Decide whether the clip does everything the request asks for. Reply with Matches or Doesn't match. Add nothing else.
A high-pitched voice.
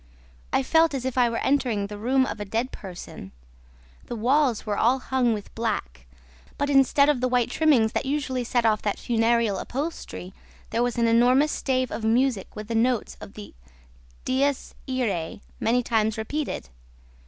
Matches